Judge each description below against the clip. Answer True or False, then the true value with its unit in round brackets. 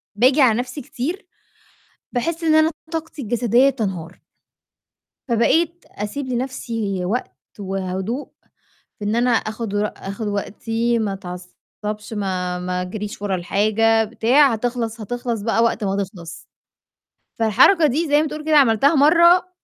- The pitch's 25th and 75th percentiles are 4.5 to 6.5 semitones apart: True (5.2 semitones)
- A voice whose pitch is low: False (225 Hz)